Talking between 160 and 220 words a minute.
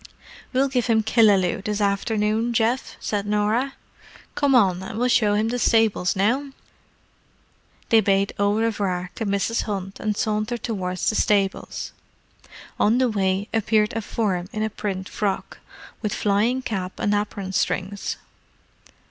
No: average, 145 wpm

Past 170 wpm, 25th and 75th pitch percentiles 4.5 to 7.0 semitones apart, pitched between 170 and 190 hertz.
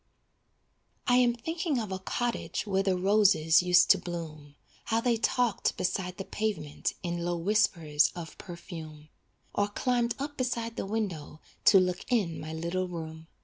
No: average, 155 wpm; average, 5.2 semitones; medium, 185 Hz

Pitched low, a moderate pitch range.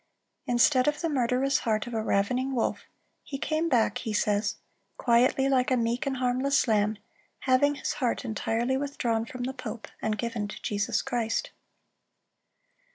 No: high, 245 Hz; average, 3.1 semitones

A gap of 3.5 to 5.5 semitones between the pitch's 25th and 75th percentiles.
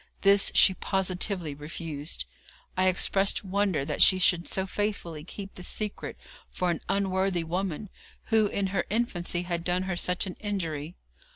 No: narrow, 2.5 semitones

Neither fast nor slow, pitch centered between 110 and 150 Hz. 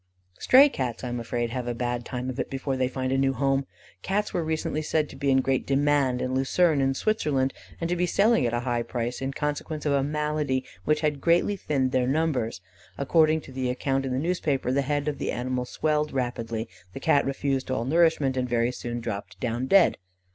No: fast, 220 wpm; low, 135 Hz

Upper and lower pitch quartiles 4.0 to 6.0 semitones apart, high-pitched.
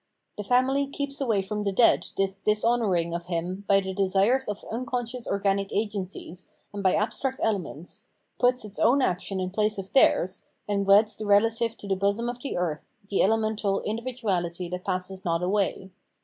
No: average, 3.3 semitones; high, 205 Hz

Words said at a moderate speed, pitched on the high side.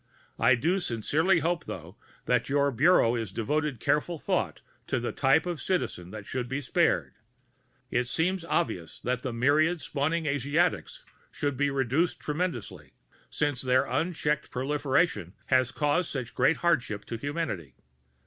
No: average, 150 wpm; medium, 140 Hz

